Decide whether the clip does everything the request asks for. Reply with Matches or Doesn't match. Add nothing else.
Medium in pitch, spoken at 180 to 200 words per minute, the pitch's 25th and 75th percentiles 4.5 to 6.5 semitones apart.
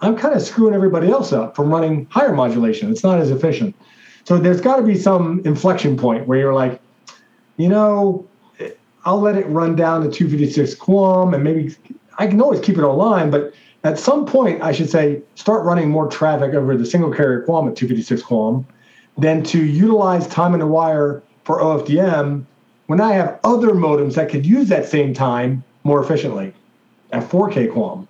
Matches